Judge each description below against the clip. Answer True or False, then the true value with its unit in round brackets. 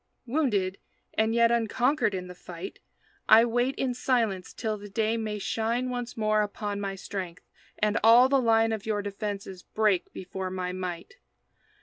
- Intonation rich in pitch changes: False (3.2 semitones)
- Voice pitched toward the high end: True (215 Hz)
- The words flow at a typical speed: True (160 wpm)